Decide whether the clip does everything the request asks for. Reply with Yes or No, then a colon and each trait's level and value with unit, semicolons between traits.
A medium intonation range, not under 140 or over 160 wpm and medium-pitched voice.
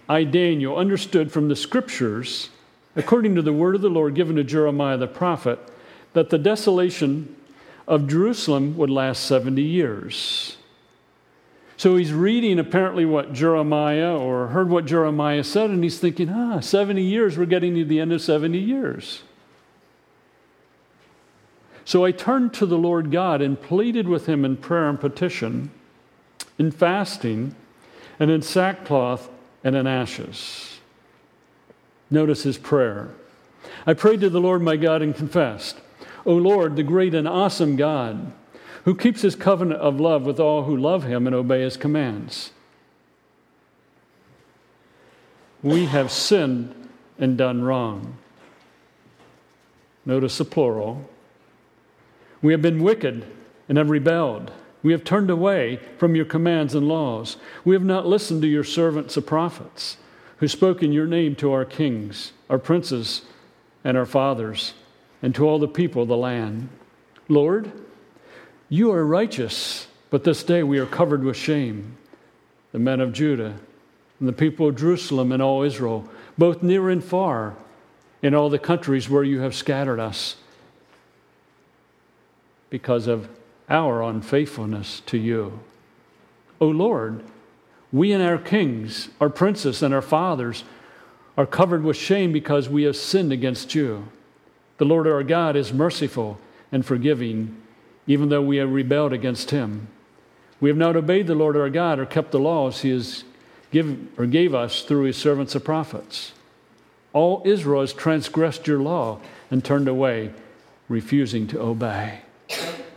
Yes: average, 4.7 semitones; average, 150 wpm; medium, 150 Hz